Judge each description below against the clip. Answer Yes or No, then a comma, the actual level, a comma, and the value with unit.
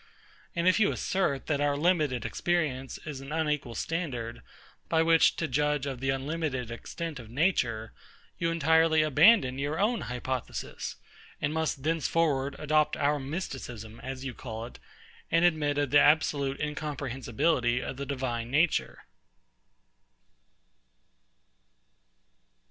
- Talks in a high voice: No, medium, 145 Hz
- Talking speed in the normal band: No, slow, 125 wpm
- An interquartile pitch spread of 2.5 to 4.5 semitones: Yes, average, 3.6 semitones